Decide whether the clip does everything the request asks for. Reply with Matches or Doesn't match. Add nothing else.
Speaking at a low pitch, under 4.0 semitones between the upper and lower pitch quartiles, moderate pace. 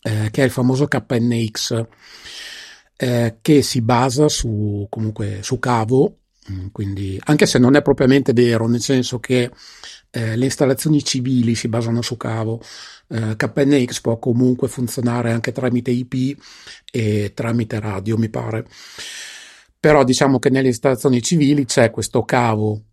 Matches